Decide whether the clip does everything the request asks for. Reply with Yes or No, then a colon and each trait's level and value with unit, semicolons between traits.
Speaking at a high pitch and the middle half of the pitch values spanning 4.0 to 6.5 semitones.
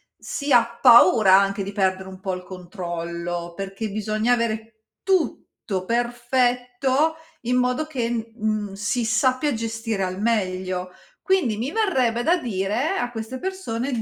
Yes: high, 225 Hz; average, 4.3 semitones